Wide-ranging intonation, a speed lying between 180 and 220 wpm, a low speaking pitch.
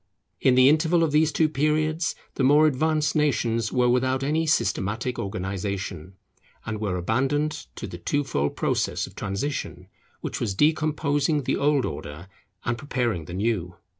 No: wide, 7.0 semitones; average, 155 wpm; low, 130 Hz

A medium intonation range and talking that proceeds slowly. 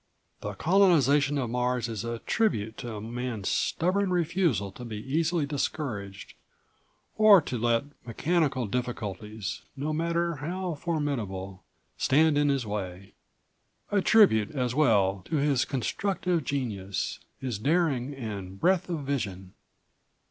No: wide, 6.9 semitones; slow, 125 wpm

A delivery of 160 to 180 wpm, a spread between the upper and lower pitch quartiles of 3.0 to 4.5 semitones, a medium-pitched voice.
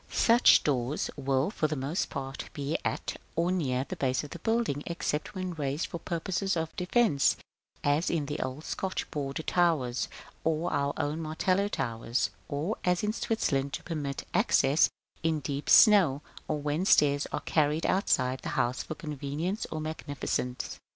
Yes: average, 165 wpm; average, 3.9 semitones; medium, 150 Hz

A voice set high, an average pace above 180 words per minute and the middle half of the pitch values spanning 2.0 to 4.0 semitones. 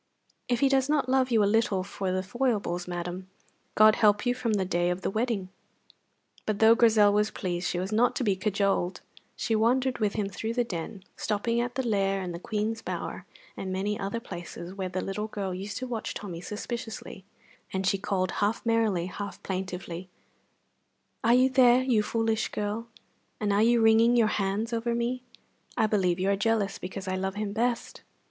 Yes: high, 210 Hz; average, 195 wpm; average, 3.5 semitones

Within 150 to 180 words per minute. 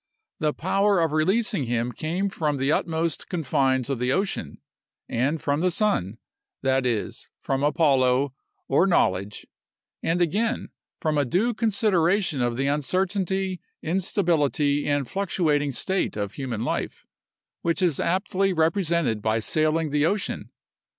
No: slow, 135 wpm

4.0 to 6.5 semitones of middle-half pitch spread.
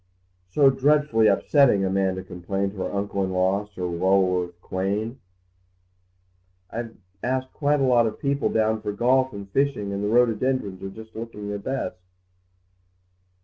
Yes: average, 4.8 semitones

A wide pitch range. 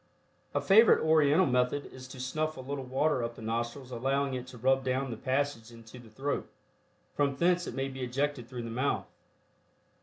No: narrow, 2.5 semitones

